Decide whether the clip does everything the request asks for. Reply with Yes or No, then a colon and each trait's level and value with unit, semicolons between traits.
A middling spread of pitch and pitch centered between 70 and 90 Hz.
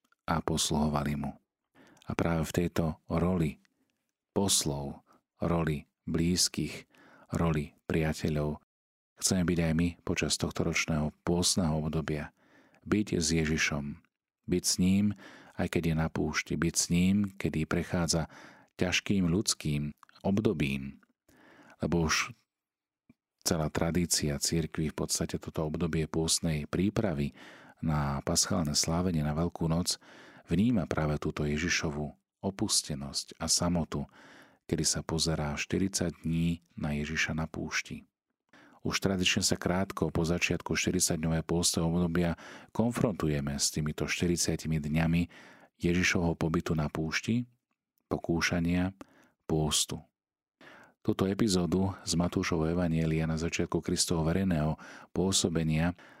No: narrow, 2.3 semitones; very low, 80 Hz